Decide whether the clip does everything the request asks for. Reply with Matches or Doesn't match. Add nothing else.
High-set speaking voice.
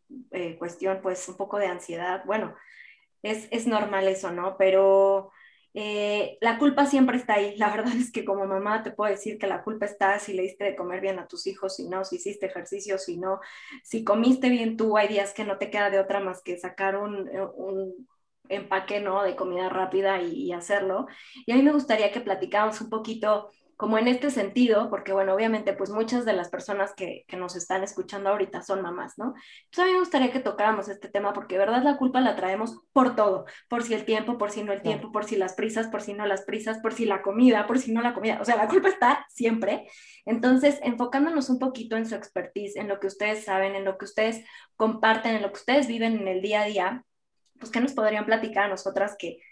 Matches